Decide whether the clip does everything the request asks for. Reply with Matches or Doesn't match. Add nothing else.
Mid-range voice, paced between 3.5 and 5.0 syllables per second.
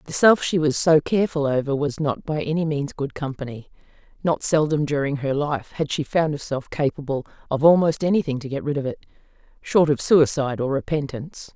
Doesn't match